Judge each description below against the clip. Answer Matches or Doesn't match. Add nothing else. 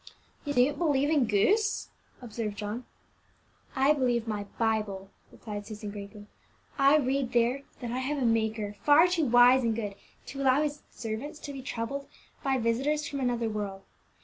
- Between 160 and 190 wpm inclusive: Matches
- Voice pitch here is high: Matches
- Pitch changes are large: Doesn't match